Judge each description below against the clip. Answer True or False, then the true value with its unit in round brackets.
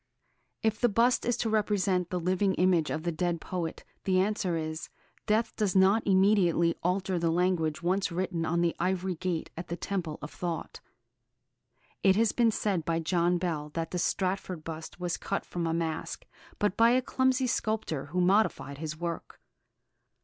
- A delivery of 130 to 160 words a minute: False (175 wpm)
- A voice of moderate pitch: True (180 Hz)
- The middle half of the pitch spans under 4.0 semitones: True (3.1 semitones)